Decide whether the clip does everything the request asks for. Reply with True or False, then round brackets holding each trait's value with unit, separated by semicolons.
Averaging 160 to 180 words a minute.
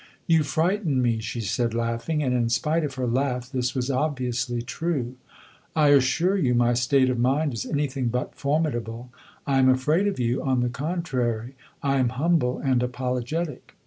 True (175 wpm)